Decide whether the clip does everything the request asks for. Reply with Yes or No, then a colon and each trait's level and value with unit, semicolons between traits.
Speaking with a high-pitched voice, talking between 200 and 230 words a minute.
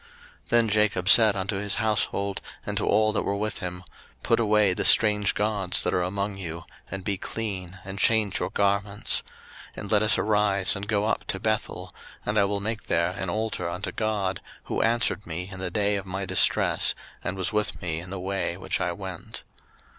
No: low, 100 Hz; fast, 205 wpm